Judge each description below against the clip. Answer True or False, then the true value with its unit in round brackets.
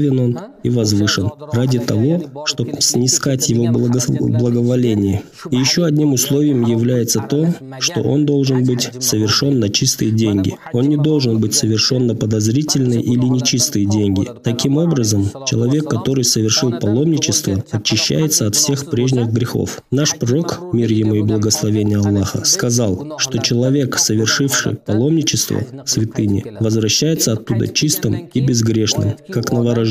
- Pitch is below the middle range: True (120 Hz)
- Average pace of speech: True (130 wpm)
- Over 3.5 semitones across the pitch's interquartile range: True (4.1 semitones)